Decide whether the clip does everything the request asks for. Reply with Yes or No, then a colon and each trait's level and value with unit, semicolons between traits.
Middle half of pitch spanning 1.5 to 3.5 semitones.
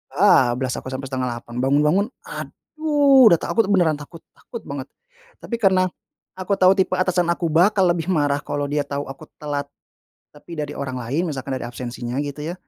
No: average, 5.2 semitones